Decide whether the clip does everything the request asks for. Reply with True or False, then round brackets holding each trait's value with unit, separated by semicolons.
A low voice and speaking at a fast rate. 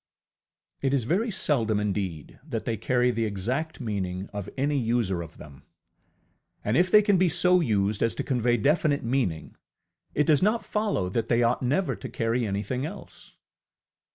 False (120 Hz; 175 wpm)